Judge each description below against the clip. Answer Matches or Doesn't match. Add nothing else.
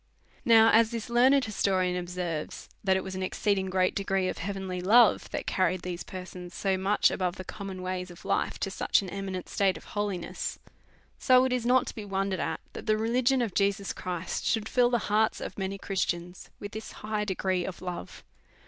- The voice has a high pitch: Matches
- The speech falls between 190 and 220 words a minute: Matches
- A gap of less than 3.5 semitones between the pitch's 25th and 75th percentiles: Matches